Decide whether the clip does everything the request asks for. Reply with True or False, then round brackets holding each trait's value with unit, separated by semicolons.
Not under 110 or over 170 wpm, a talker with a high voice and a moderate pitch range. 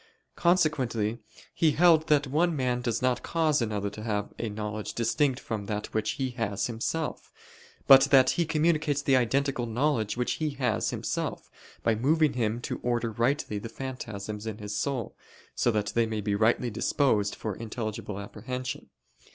False (160 wpm; 120 Hz; 4.6 semitones)